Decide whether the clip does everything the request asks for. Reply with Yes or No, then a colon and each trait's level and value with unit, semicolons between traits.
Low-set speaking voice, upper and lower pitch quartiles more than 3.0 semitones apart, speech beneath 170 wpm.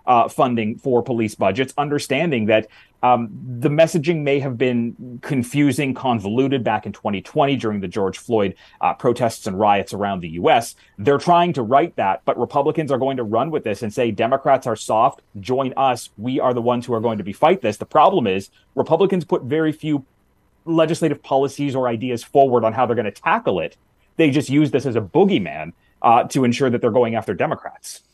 No: low, 125 Hz; average, 3.9 semitones; average, 200 wpm